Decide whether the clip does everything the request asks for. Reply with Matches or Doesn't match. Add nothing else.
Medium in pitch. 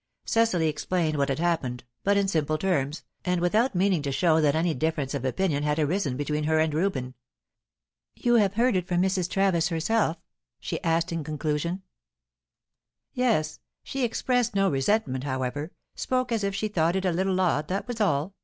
Matches